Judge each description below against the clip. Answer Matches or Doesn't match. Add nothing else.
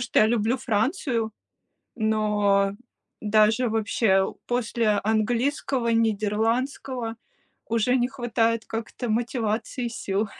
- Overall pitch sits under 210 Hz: Doesn't match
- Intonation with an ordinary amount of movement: Doesn't match